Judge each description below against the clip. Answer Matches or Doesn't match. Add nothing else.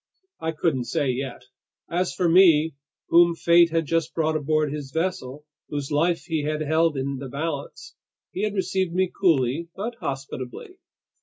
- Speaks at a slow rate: Doesn't match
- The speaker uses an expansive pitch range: Doesn't match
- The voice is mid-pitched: Matches